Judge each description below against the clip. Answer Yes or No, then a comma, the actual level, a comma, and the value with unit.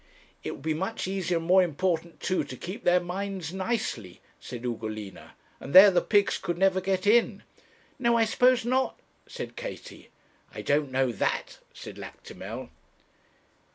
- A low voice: No, medium, 185 Hz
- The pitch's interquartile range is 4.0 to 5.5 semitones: Yes, average, 4.4 semitones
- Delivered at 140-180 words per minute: Yes, average, 155 wpm